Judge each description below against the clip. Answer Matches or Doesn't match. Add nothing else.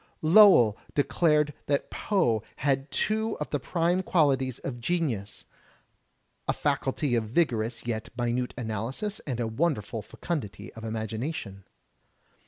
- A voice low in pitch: Matches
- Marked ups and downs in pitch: Matches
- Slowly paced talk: Matches